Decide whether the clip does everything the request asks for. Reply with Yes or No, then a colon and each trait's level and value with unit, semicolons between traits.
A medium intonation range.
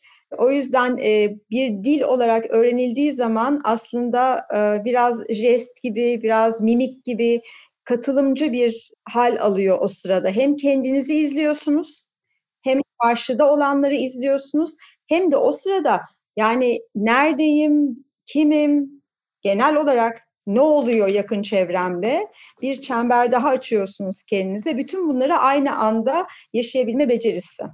Yes: average, 3.8 semitones